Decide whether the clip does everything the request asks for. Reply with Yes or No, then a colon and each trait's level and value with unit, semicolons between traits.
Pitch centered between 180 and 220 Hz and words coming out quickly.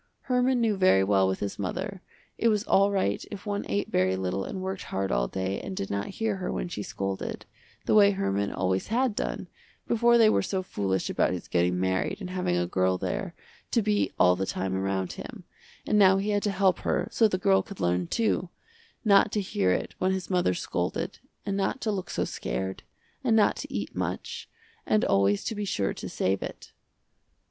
Yes: medium, 185 Hz; fast, 210 wpm